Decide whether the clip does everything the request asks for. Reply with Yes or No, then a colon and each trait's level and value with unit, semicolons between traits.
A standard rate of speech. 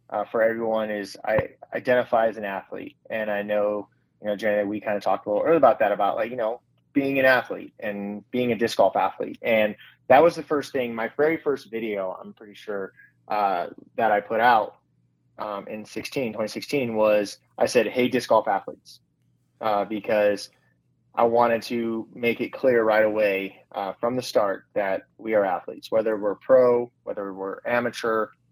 Yes: average, 190 wpm